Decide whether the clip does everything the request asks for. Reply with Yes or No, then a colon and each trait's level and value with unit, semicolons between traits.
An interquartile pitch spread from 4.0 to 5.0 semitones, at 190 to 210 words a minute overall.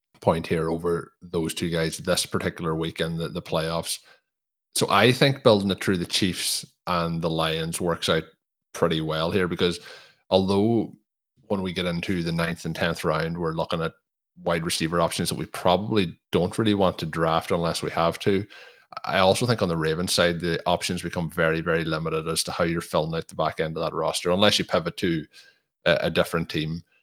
No: narrow, 2.4 semitones; average, 200 wpm